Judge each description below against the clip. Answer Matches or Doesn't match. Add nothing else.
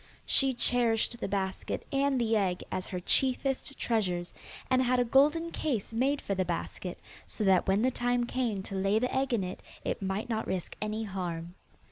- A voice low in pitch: Doesn't match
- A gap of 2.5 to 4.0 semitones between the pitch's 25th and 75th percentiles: Doesn't match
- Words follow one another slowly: Doesn't match